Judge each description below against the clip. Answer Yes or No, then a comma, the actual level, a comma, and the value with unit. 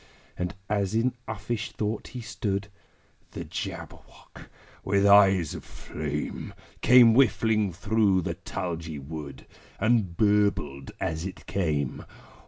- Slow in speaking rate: Yes, slow, 115 wpm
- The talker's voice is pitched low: Yes, low, 100 Hz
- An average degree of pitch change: Yes, average, 4.9 semitones